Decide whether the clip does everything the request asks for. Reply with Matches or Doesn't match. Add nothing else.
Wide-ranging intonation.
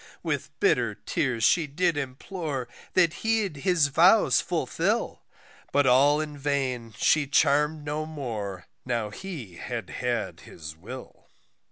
Doesn't match